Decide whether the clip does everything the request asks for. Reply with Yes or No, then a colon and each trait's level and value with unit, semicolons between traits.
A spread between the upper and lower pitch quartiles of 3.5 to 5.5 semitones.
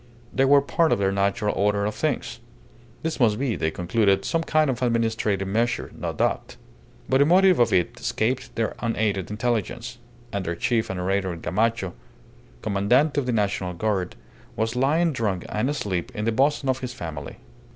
Yes: average, 4.6 semitones